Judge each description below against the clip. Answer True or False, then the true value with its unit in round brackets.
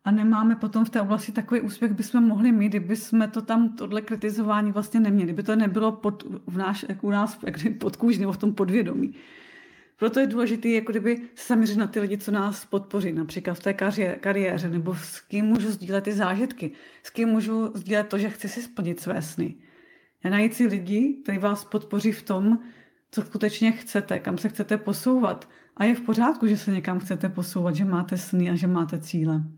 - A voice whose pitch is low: False (210 Hz)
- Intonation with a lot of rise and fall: False (2.4 semitones)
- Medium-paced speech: False (205 wpm)